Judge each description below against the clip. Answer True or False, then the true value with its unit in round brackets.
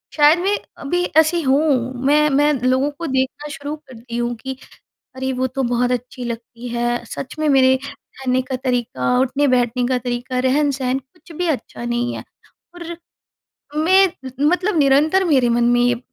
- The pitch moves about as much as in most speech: True (3.3 semitones)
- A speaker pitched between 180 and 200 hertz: False (260 Hz)